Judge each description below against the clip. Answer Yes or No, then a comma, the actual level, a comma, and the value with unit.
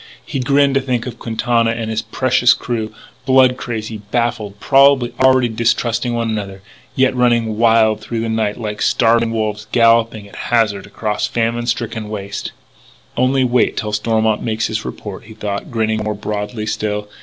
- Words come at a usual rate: Yes, average, 165 wpm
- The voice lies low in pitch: Yes, low, 115 Hz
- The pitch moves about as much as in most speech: No, narrow, 2.1 semitones